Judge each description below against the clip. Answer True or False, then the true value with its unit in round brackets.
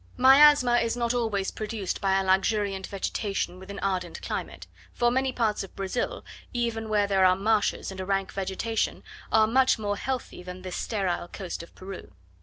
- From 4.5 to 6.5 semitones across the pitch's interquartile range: False (3.5 semitones)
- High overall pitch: True (205 Hz)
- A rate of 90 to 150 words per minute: False (180 wpm)